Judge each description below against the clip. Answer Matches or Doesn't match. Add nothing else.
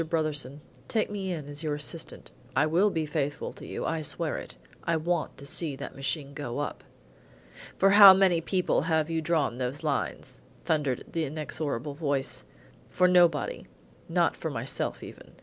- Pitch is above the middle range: Doesn't match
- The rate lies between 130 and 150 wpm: Doesn't match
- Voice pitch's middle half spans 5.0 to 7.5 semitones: Doesn't match